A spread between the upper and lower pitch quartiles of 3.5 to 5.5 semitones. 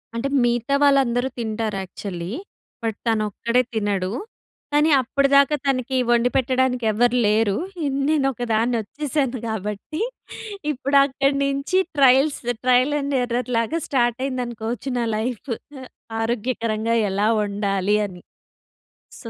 Yes: average, 3.8 semitones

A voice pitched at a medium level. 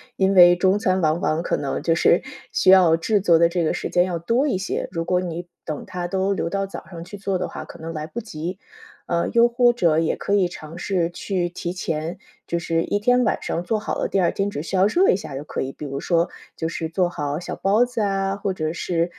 Yes: medium, 180 Hz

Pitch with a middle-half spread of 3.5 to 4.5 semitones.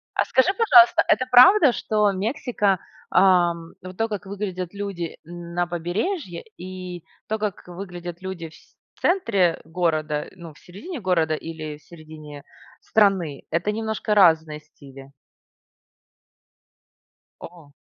Yes: average, 4.2 semitones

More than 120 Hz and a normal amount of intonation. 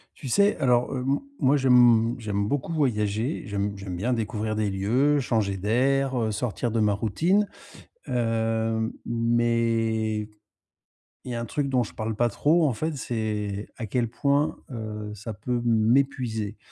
No: low, 115 Hz; average, 3.1 semitones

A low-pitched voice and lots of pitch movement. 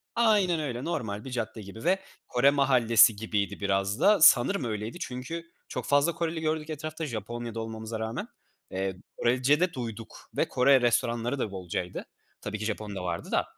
Yes: low, 120 Hz; wide, 5.7 semitones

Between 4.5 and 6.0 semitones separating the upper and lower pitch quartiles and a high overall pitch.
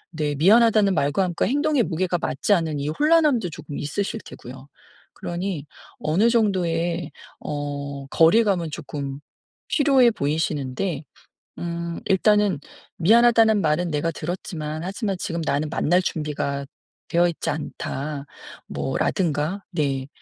No: average, 5.2 semitones; medium, 170 Hz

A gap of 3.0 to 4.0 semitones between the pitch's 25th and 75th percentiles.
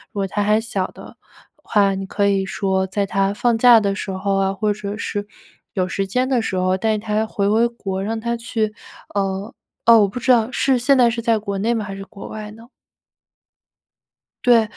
No: narrow, 2.6 semitones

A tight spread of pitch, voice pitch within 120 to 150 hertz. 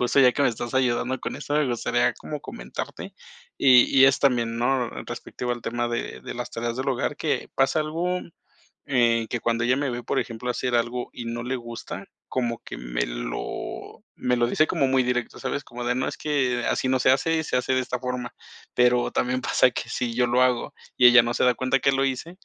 Yes: narrow, 1.8 semitones; low, 125 Hz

